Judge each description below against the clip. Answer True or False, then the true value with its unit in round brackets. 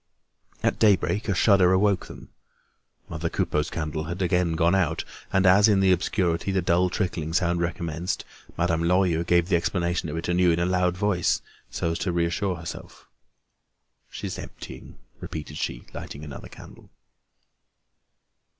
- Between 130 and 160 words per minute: True (150 wpm)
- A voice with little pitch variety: True (1.9 semitones)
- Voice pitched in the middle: False (85 Hz)